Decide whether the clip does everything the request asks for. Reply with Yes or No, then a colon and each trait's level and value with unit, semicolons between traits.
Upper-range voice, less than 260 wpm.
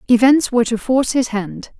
Yes: high, 240 Hz; average, 200 wpm